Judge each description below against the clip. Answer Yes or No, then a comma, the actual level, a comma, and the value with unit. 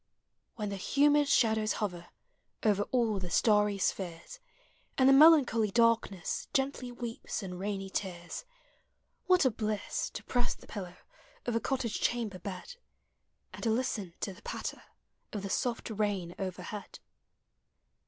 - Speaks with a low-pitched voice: No, high, 215 Hz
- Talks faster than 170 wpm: No, average, 140 wpm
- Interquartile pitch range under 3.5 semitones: No, average, 3.9 semitones